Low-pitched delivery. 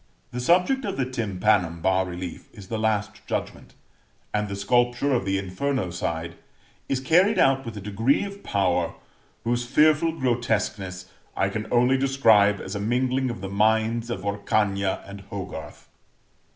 Yes: low, 110 Hz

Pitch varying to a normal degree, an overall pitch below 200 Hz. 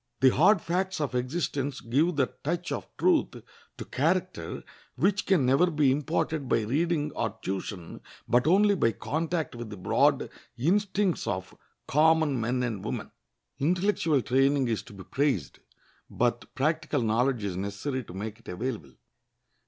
No: wide, 6.0 semitones; low, 135 Hz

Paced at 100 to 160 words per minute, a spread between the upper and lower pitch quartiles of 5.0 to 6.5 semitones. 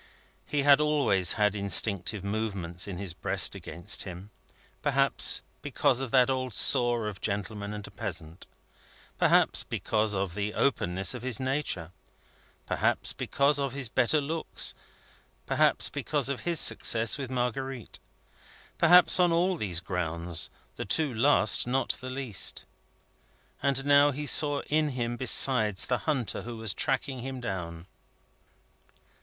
Yes: average, 140 wpm; wide, 5.6 semitones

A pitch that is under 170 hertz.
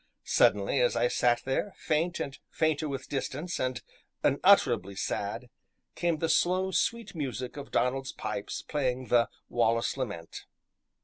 Yes: low, 135 Hz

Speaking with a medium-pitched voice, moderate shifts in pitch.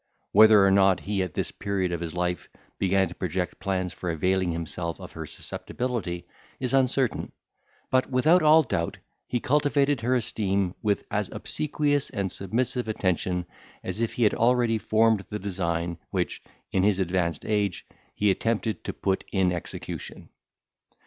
No: low, 100 Hz; average, 4.7 semitones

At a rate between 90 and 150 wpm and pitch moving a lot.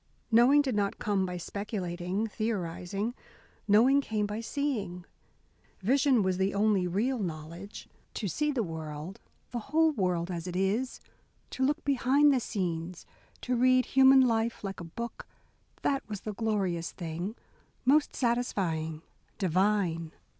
Yes: average, 140 wpm; wide, 5.7 semitones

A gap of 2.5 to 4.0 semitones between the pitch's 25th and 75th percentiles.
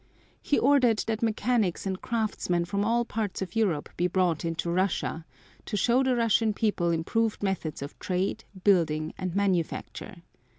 No: average, 4.6 semitones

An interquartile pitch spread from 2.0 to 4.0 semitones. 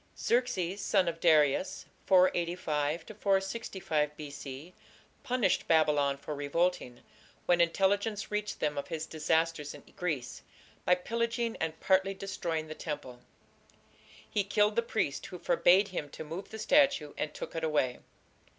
No: average, 4.7 semitones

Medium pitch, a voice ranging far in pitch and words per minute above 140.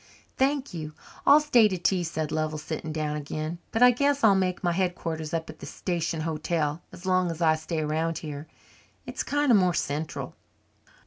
No: medium, 165 Hz; average, 3.3 semitones; average, 190 wpm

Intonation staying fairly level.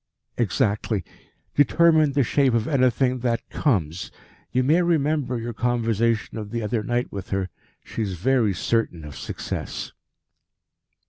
No: average, 4.1 semitones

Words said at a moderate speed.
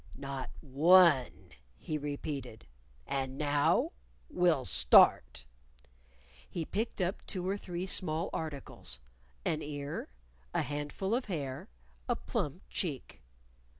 No: slow, 110 wpm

